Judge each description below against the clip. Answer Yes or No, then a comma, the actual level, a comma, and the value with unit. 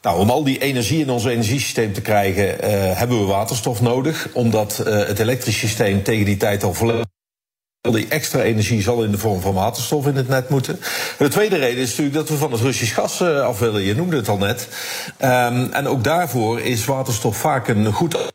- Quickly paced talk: Yes, fast, 215 wpm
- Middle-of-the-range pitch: No, low, 120 Hz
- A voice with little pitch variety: No, average, 3.9 semitones